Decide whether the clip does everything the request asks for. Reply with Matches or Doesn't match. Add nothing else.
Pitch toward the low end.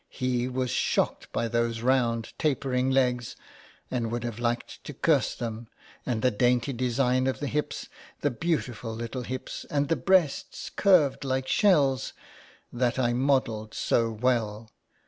Matches